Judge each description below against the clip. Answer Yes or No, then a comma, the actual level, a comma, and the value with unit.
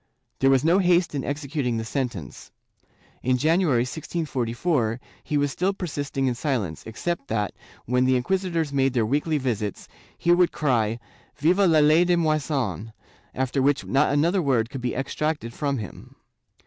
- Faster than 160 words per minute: No, average, 155 wpm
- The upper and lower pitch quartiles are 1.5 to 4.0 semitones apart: No, average, 4.6 semitones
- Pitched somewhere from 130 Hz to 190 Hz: Yes, medium, 140 Hz